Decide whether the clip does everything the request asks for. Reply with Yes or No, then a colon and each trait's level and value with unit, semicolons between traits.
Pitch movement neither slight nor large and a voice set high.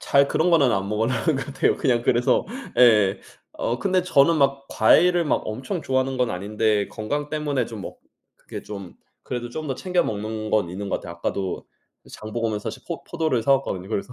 No: average, 4.7 semitones; low, 120 Hz